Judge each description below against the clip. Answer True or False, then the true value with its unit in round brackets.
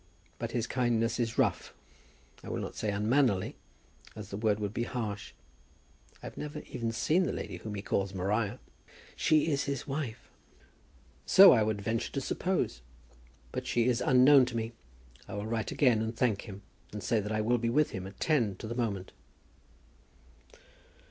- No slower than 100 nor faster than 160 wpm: False (180 wpm)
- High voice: False (115 Hz)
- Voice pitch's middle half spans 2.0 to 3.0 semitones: False (3.4 semitones)